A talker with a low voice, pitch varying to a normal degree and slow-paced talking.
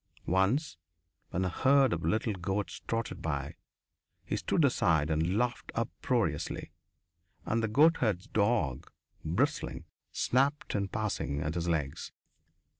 No: low, 100 Hz; wide, 6.0 semitones; slow, 120 wpm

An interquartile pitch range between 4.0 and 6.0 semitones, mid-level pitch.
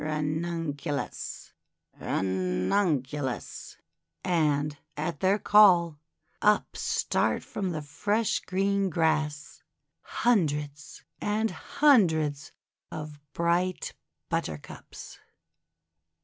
Yes: average, 4.5 semitones; medium, 160 Hz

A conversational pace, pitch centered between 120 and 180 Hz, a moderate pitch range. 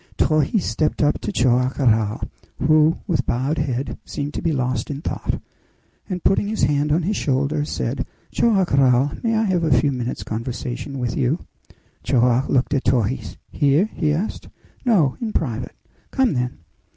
Yes: average, 165 wpm; medium, 140 Hz; average, 4.3 semitones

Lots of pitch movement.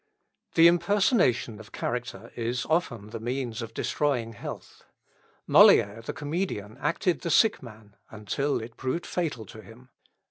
Yes: wide, 6.0 semitones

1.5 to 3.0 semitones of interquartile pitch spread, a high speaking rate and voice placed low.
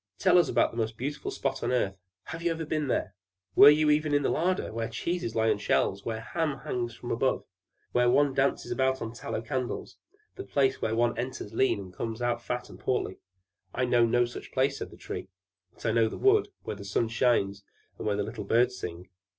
No: average, 3.8 semitones; fast, 230 wpm; low, 120 Hz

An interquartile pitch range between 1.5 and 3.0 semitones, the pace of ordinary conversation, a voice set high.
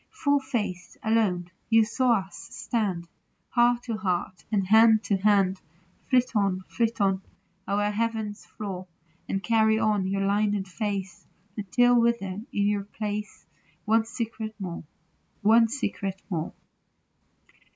No: average, 2.7 semitones; slow, 130 wpm; high, 210 Hz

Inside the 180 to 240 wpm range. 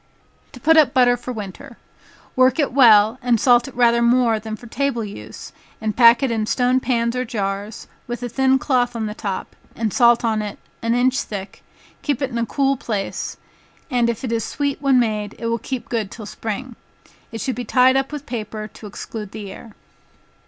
Yes: fast, 205 wpm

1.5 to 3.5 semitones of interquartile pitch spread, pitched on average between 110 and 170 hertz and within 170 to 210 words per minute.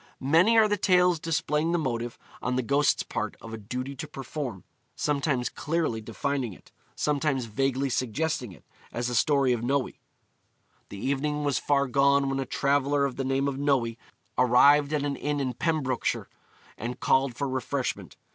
Yes: average, 2.8 semitones; medium, 140 Hz; average, 175 wpm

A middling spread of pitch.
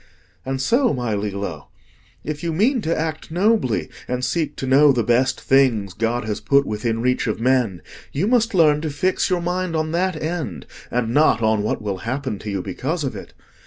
No: wide, 6.5 semitones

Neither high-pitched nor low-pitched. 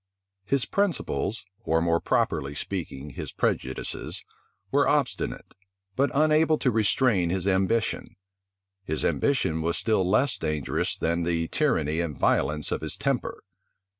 No: very low, 95 Hz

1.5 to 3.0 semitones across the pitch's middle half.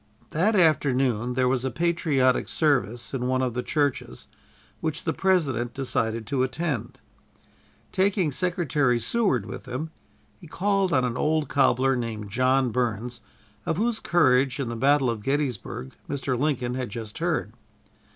No: average, 4.3 semitones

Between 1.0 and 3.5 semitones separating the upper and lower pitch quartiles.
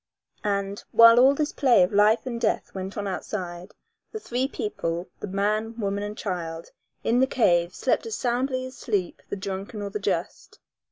No: average, 3.9 semitones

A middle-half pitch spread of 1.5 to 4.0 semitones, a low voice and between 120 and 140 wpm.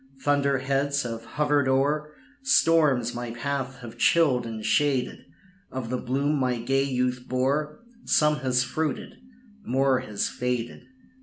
Yes: narrow, 2.6 semitones; low, 130 Hz; slow, 135 wpm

